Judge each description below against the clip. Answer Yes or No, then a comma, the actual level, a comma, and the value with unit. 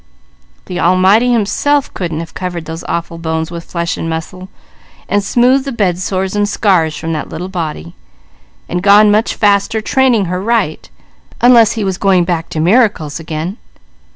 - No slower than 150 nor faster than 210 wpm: Yes, average, 165 wpm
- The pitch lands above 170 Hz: Yes, medium, 185 Hz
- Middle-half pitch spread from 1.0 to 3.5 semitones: No, average, 4.1 semitones